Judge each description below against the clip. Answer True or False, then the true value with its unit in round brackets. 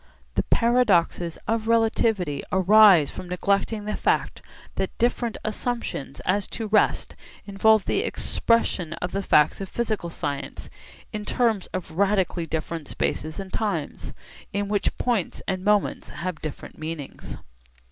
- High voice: True (195 Hz)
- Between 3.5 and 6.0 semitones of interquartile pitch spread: True (4.4 semitones)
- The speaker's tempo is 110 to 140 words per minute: True (135 wpm)